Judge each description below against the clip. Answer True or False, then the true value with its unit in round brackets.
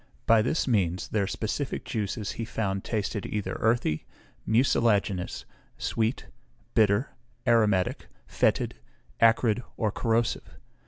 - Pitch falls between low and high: False (110 Hz)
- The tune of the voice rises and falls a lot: False (2.4 semitones)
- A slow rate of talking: True (105 wpm)